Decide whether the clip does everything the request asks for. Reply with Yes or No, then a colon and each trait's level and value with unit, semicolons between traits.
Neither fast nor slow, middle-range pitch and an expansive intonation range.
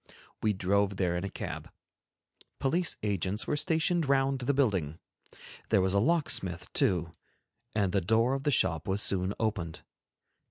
No: average, 155 wpm; low, 100 Hz; wide, 6.5 semitones